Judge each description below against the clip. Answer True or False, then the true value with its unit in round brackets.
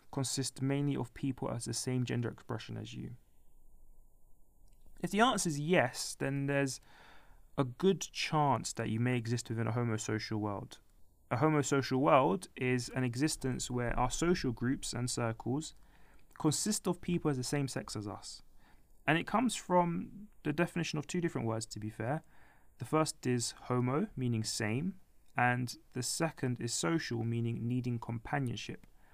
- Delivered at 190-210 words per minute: False (160 wpm)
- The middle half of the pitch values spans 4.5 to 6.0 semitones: True (4.8 semitones)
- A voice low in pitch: True (125 Hz)